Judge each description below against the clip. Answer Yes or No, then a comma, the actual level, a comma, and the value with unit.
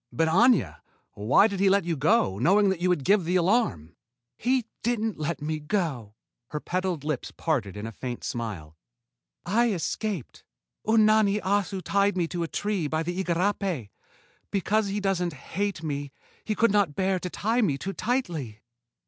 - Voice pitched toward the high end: No, medium, 180 Hz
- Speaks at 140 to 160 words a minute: No, average, 170 wpm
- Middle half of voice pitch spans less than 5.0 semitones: No, wide, 5.6 semitones